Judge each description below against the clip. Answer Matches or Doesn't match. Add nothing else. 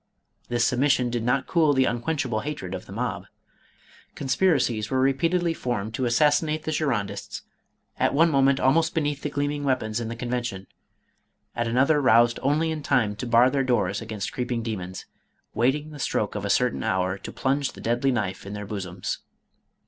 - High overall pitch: Doesn't match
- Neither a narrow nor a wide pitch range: Matches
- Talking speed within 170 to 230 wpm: Matches